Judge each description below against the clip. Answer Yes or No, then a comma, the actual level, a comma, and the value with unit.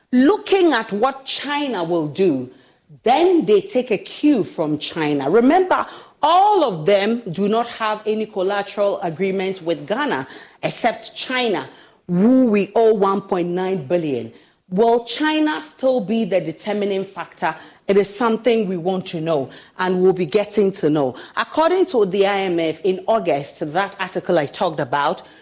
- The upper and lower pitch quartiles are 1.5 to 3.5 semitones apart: No, average, 5.1 semitones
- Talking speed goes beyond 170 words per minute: No, average, 150 wpm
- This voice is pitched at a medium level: No, high, 200 Hz